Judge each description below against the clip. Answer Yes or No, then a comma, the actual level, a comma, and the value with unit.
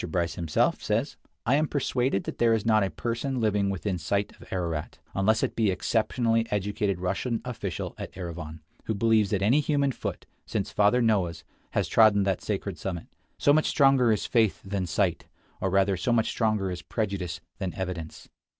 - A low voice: Yes, low, 100 Hz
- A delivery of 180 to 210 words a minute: Yes, average, 185 wpm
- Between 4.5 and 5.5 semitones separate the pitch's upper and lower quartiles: No, average, 3.6 semitones